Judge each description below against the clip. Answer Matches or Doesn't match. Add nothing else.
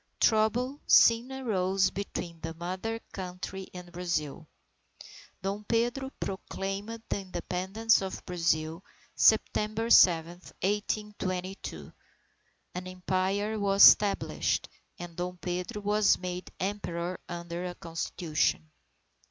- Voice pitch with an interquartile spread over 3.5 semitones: Doesn't match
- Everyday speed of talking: Doesn't match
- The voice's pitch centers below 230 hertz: Matches